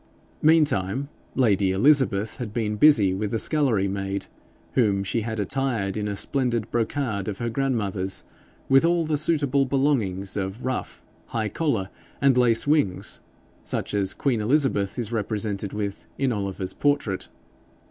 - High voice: No, low, 110 Hz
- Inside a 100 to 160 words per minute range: Yes, average, 140 wpm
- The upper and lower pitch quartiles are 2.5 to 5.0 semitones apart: No, wide, 5.4 semitones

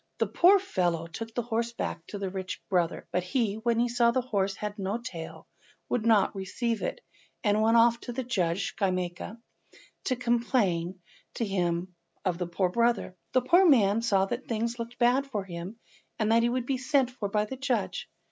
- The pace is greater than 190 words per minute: Yes, average, 200 wpm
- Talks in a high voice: Yes, high, 225 Hz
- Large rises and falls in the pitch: No, average, 4.1 semitones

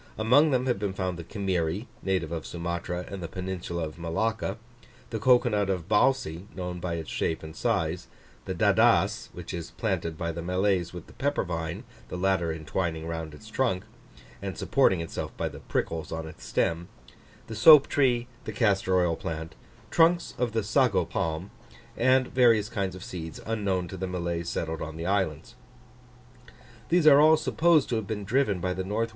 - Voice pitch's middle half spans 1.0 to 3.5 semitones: No, average, 5.0 semitones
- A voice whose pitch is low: Yes, very low, 95 Hz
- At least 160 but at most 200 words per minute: Yes, average, 185 wpm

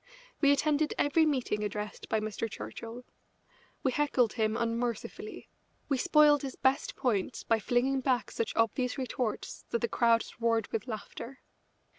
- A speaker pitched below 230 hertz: No, high, 245 Hz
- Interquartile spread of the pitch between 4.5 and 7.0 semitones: No, average, 3.3 semitones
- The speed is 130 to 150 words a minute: Yes, average, 145 wpm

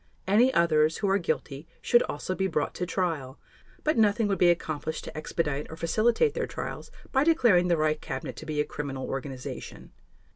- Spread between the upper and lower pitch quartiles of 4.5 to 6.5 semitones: Yes, average, 5.2 semitones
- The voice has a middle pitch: Yes, medium, 170 Hz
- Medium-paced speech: Yes, average, 185 wpm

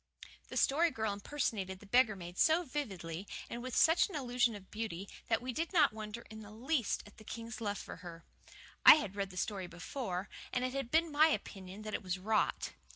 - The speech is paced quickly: Yes, fast, 215 wpm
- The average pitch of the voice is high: Yes, high, 220 Hz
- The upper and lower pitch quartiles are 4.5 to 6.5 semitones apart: Yes, average, 5.0 semitones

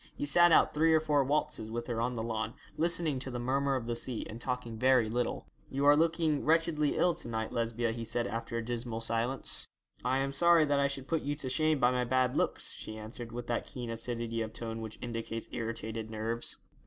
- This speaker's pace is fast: Yes, fast, 225 wpm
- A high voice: No, low, 125 Hz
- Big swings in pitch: No, average, 3.8 semitones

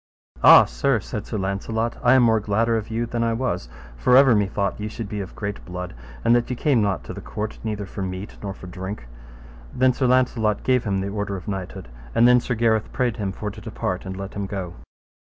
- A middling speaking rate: No, fast, 240 wpm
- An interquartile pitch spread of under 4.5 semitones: Yes, average, 3.2 semitones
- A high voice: No, low, 105 Hz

